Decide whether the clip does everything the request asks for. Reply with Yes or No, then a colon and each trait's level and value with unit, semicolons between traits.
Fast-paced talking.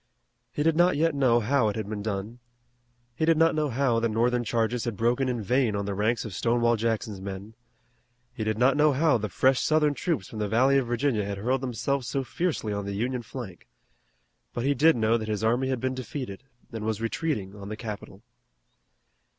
Yes: fast, 210 wpm